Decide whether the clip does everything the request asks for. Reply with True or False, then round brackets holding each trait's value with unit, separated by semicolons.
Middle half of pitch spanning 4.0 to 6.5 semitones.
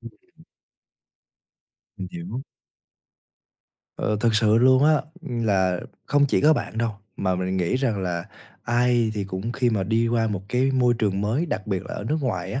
True (4.6 semitones)